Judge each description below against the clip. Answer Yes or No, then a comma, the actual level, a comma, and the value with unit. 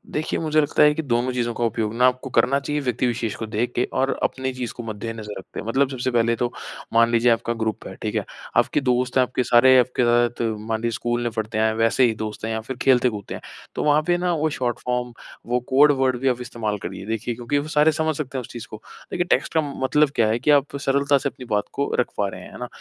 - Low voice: Yes, low, 125 Hz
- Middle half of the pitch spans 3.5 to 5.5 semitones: No, average, 2.8 semitones